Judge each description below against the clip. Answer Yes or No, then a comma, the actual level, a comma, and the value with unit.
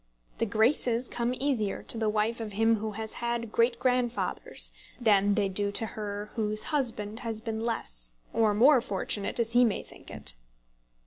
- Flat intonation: Yes, narrow, 2.2 semitones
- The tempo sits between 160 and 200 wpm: Yes, average, 175 wpm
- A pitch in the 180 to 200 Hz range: No, high, 225 Hz